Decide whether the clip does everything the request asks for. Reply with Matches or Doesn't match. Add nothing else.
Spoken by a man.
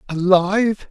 Matches